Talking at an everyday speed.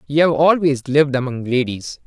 Yes: average, 175 wpm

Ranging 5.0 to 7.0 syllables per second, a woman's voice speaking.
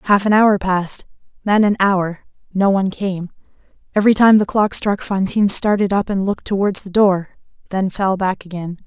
Yes: 5.3 syllables/s; female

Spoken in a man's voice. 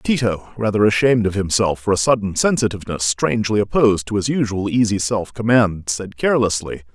Yes: male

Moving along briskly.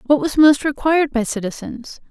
No: average, 170 wpm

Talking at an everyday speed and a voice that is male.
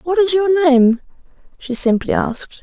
No: average, 160 wpm; female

